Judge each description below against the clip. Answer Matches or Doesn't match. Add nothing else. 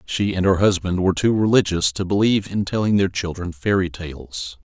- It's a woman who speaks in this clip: Doesn't match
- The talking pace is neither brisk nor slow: Matches